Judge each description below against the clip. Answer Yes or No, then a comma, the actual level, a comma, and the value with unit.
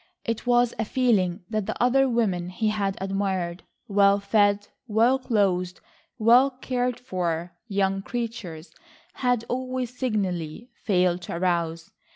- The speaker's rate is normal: No, slow, 120 wpm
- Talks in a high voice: Yes, high, 205 Hz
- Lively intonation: No, average, 4.9 semitones